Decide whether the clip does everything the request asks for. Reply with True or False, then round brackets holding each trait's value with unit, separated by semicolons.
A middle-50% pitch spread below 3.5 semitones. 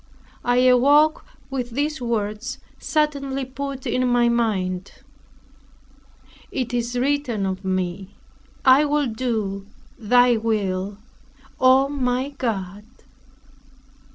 False (4.6 semitones)